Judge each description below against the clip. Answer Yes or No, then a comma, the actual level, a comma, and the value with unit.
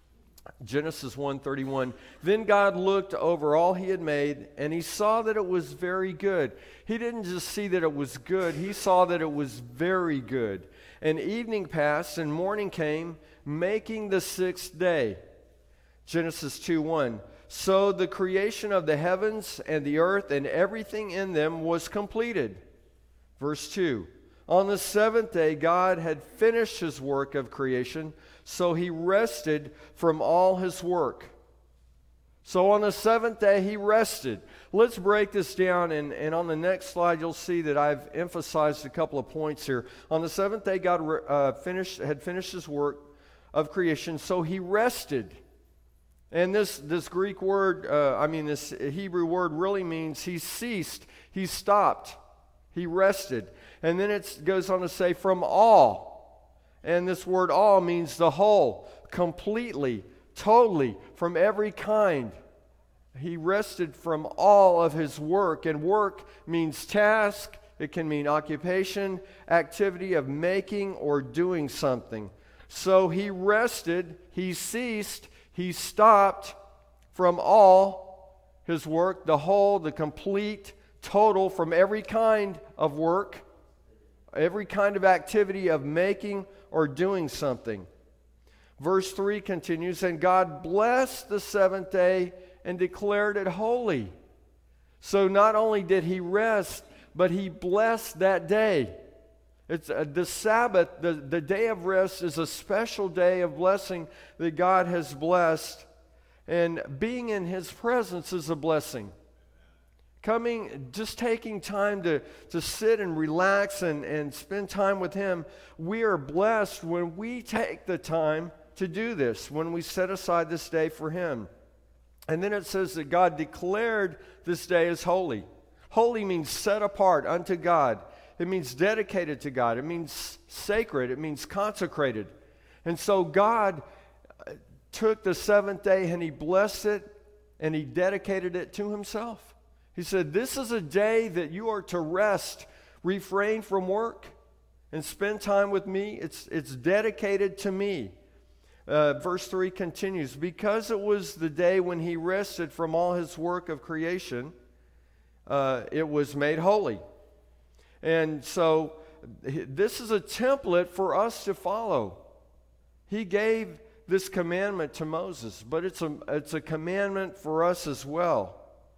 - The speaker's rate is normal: Yes, average, 150 wpm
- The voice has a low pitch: No, medium, 180 Hz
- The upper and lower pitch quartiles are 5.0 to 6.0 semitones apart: No, average, 4.3 semitones